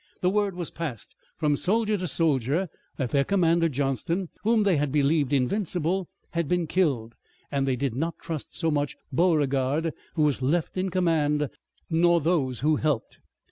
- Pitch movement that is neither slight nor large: Yes, average, 4.0 semitones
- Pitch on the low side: No, medium, 160 Hz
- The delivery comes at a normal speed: Yes, average, 165 wpm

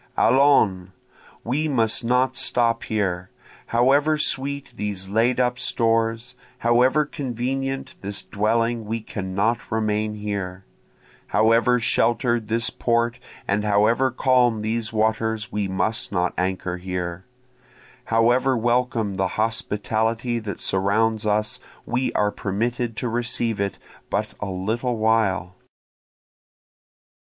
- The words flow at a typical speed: No, slow, 110 wpm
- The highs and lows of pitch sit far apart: No, average, 2.9 semitones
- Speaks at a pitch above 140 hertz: No, low, 115 Hz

